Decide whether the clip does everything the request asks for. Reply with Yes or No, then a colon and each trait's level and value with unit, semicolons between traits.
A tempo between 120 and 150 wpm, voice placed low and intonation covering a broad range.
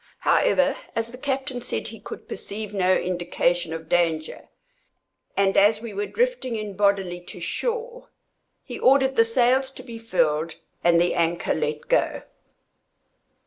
No: average, 145 wpm; high, 205 Hz; wide, 6.8 semitones